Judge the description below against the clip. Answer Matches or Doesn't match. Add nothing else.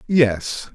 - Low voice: Matches